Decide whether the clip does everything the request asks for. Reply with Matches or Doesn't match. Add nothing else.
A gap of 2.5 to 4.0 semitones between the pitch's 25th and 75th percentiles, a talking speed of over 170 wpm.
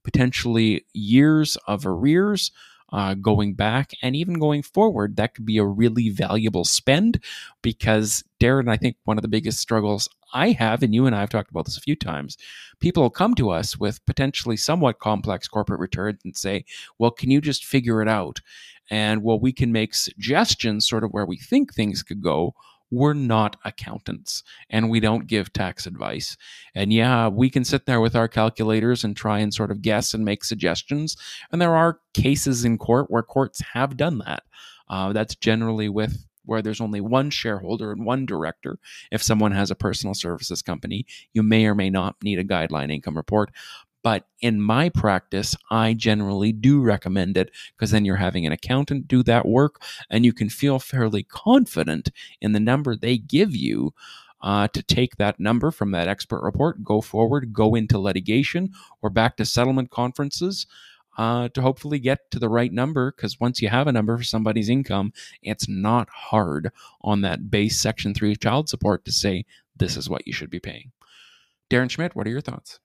Matches